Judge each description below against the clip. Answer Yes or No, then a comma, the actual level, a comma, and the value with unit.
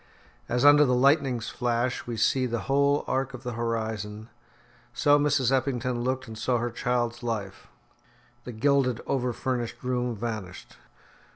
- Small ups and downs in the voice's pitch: Yes, narrow, 2.2 semitones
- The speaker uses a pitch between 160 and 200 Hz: No, low, 125 Hz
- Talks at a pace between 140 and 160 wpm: Yes, average, 150 wpm